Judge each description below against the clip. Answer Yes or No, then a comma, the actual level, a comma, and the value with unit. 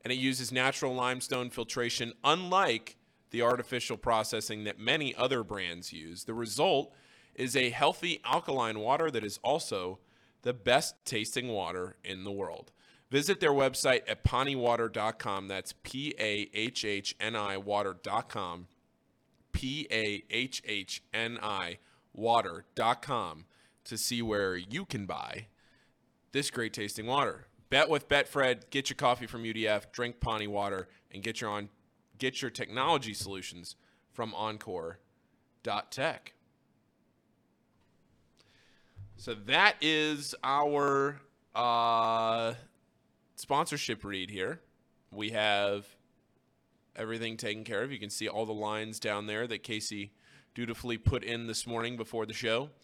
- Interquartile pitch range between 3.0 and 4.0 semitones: Yes, average, 3.5 semitones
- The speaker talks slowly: Yes, slow, 120 wpm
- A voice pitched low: Yes, low, 115 Hz